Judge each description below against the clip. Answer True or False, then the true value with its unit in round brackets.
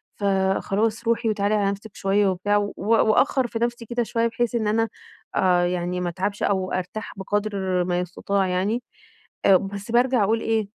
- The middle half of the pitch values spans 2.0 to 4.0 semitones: True (2.9 semitones)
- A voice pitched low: False (205 Hz)